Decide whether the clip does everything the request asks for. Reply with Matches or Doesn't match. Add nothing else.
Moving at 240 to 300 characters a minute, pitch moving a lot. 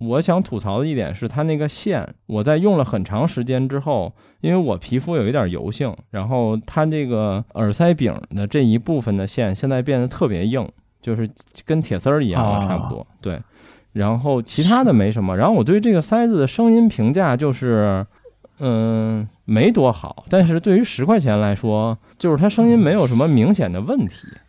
Matches